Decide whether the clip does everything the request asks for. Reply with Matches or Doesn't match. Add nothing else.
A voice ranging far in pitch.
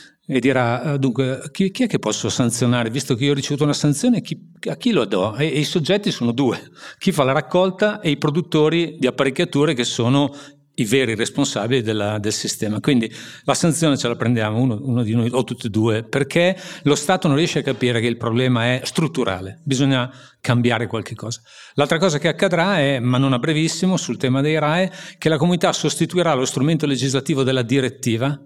Doesn't match